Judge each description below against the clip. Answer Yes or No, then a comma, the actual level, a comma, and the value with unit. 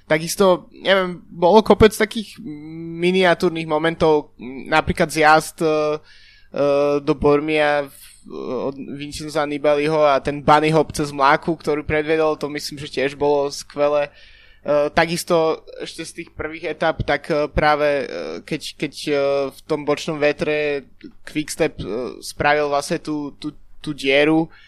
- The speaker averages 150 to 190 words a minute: No, average, 140 wpm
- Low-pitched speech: No, medium, 150 Hz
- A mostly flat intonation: Yes, narrow, 2.0 semitones